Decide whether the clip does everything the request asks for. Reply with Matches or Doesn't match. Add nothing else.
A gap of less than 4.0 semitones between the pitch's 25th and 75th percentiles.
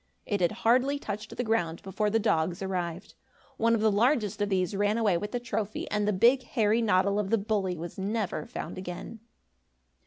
Matches